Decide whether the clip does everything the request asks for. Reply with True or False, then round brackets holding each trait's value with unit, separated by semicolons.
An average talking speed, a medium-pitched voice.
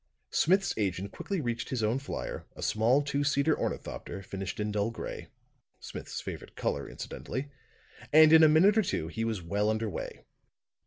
False (170 wpm; 115 Hz)